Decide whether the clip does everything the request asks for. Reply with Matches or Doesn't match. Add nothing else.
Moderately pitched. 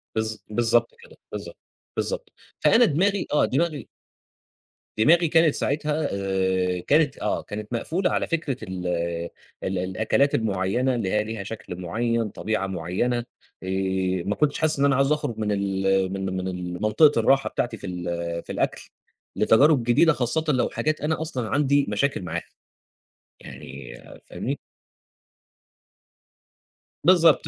Doesn't match